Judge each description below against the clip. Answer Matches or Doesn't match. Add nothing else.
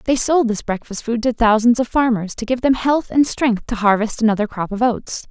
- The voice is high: Matches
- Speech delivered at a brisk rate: Matches